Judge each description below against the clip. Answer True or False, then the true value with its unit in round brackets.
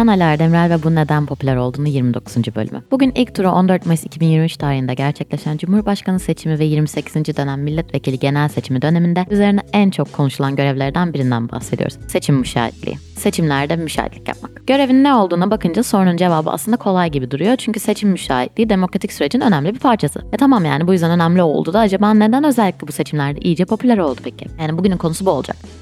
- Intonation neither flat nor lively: False (6.1 semitones)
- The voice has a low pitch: False (165 Hz)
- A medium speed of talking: False (180 wpm)